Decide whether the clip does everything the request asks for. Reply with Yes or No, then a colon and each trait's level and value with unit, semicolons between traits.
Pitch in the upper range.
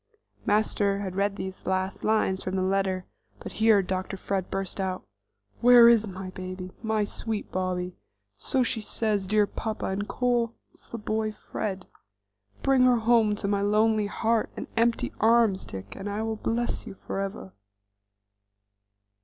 Yes: high, 205 Hz